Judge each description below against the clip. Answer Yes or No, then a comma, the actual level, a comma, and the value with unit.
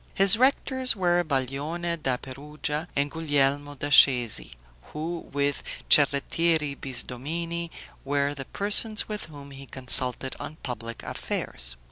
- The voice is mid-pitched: Yes, medium, 145 Hz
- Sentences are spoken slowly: Yes, slow, 120 wpm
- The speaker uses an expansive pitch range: No, average, 3.8 semitones